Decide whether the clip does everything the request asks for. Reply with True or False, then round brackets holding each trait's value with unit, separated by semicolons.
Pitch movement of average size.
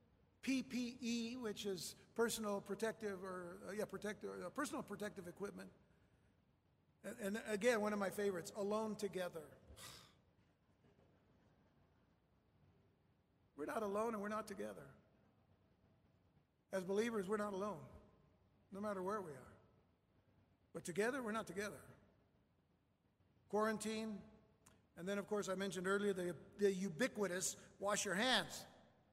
False (8.5 semitones)